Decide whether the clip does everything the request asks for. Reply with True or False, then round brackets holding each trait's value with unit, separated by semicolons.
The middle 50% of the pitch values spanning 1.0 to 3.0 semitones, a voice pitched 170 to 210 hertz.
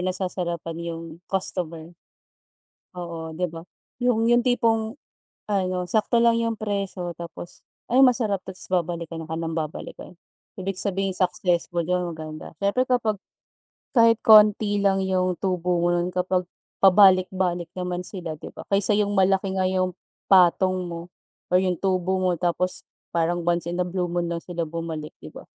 True (2.4 semitones; 185 Hz)